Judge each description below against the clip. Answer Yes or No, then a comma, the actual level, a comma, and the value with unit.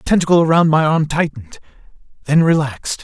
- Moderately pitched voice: Yes, medium, 155 Hz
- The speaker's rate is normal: Yes, average, 160 wpm